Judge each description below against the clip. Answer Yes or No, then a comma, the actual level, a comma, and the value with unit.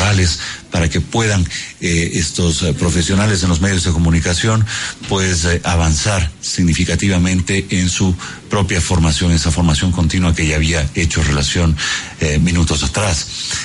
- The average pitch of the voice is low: Yes, very low, 90 Hz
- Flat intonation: Yes, narrow, 2.1 semitones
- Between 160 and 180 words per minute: No, average, 135 wpm